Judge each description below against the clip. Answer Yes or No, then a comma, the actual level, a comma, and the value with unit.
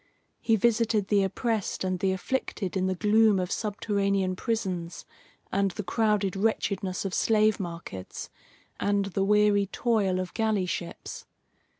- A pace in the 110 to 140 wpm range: Yes, slow, 135 wpm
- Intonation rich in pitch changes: No, narrow, 2.6 semitones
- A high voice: Yes, high, 200 Hz